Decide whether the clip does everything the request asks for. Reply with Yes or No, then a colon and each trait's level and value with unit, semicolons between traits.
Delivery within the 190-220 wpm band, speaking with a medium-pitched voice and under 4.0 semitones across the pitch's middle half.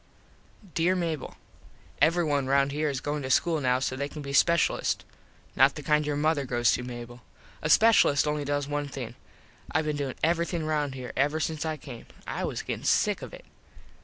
Yes: average, 195 wpm; medium, 145 Hz; average, 2.7 semitones